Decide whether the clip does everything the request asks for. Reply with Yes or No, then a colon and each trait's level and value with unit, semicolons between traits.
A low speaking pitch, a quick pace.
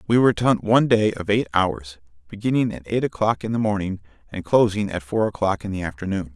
Yes: low, 100 Hz; fast, 225 wpm